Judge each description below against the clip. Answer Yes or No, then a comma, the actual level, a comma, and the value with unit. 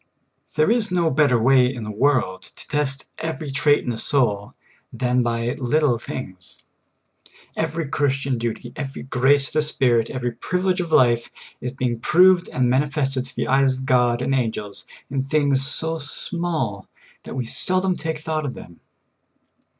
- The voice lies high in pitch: No, low, 135 Hz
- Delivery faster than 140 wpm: Yes, average, 165 wpm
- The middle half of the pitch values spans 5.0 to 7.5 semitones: No, average, 3.9 semitones